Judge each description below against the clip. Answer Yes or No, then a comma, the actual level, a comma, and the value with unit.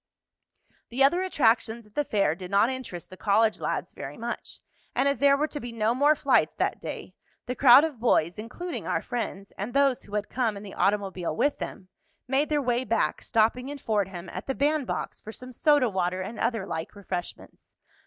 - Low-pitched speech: No, high, 230 Hz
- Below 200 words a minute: No, fast, 205 wpm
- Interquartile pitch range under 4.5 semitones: No, wide, 5.4 semitones